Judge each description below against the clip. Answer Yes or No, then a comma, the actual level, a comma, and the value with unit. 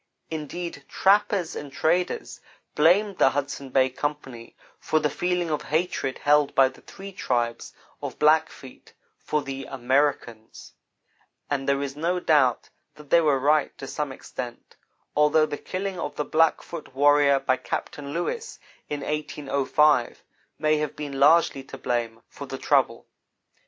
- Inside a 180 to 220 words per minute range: No, average, 145 wpm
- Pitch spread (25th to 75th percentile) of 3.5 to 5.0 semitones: No, average, 2.8 semitones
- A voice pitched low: No, medium, 145 Hz